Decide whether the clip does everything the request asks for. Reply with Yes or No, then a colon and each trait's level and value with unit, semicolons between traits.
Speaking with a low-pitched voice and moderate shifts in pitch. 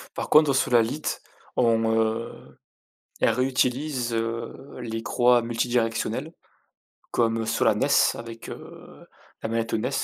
No: low, 115 Hz; narrow, 1.8 semitones